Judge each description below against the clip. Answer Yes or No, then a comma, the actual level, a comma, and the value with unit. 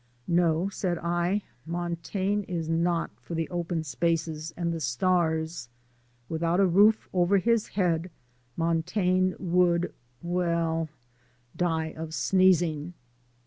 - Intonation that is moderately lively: No, narrow, 1.9 semitones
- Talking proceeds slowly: Yes, slow, 110 wpm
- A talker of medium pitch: Yes, medium, 170 Hz